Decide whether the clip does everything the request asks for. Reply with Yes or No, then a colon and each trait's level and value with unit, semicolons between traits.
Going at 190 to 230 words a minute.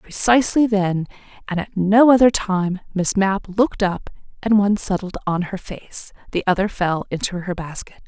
No: average, 170 wpm